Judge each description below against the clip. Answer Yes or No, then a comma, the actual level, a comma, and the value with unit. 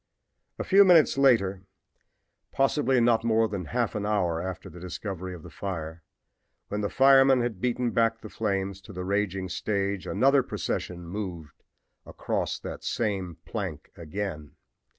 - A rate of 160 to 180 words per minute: No, average, 150 wpm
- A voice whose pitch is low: Yes, low, 100 Hz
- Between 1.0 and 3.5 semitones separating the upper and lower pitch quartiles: No, average, 4.4 semitones